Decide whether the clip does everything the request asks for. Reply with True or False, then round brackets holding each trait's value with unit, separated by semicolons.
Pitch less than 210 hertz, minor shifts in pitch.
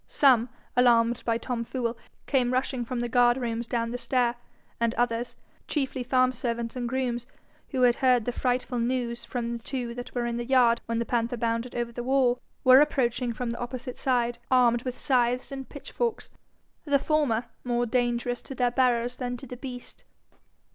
False (245 Hz; 1.3 semitones)